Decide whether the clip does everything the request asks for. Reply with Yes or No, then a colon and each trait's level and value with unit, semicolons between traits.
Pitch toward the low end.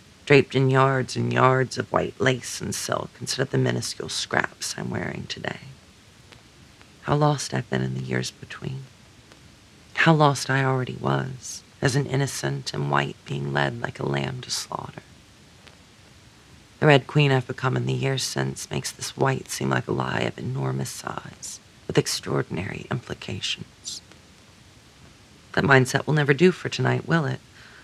Yes: low, 125 Hz